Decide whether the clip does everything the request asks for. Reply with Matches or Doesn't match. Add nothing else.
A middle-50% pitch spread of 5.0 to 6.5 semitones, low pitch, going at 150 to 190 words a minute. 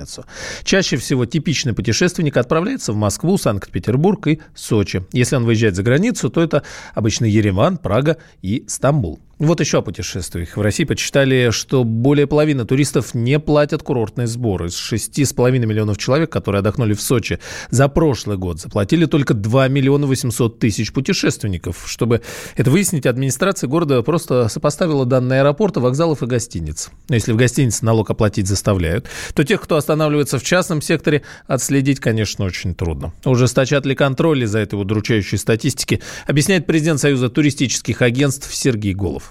Matches